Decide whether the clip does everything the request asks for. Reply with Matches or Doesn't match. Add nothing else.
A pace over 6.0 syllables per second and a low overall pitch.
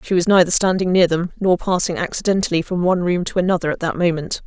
Doesn't match